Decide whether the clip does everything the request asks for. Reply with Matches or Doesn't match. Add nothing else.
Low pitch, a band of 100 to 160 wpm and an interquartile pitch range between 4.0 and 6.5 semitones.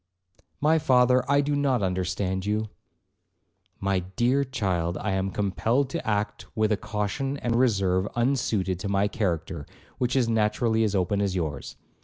Matches